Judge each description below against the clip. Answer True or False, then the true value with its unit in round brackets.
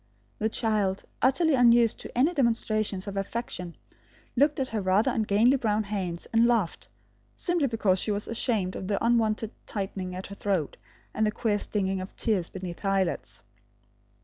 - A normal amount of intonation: True (3.4 semitones)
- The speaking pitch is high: True (210 Hz)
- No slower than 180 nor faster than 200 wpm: False (165 wpm)